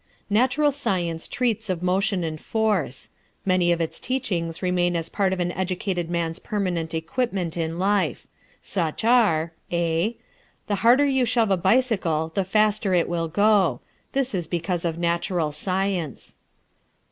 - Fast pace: No, average, 145 wpm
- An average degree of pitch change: Yes, average, 4.1 semitones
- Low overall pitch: No, medium, 185 Hz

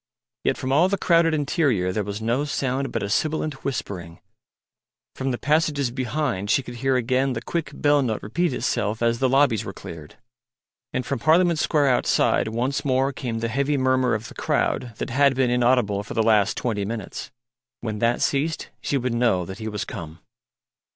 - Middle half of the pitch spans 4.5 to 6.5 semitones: No, average, 4.1 semitones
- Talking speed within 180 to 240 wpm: Yes, average, 190 wpm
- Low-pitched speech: Yes, low, 125 Hz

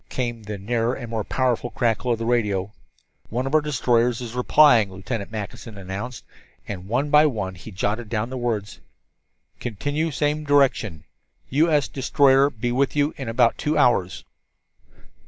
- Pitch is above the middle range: No, low, 120 Hz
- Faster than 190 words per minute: No, average, 160 wpm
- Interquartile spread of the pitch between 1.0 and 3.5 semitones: No, average, 4.0 semitones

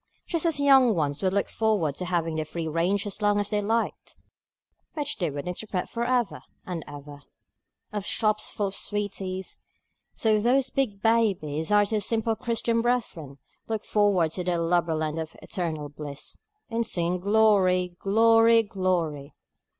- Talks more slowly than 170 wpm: Yes, average, 160 wpm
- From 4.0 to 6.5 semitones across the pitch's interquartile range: Yes, average, 5.0 semitones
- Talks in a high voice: Yes, high, 200 Hz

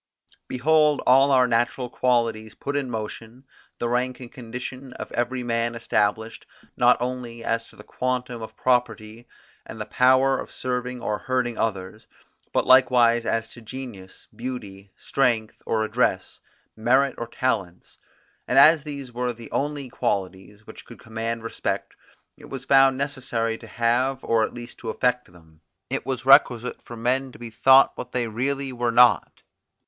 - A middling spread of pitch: No, narrow, 2.3 semitones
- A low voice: Yes, low, 120 Hz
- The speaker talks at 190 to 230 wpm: No, average, 160 wpm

